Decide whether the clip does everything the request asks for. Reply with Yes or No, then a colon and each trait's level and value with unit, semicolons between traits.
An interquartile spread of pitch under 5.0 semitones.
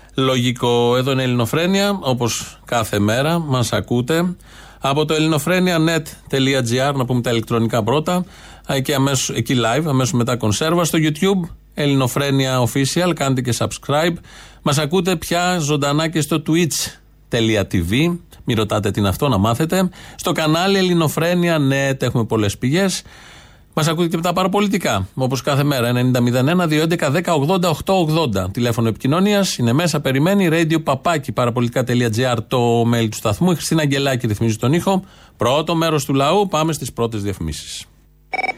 No: wide, 5.4 semitones